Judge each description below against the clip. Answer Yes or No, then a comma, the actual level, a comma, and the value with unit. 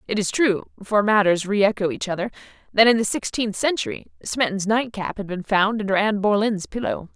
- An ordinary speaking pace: Yes, average, 195 wpm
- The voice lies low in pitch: No, high, 205 Hz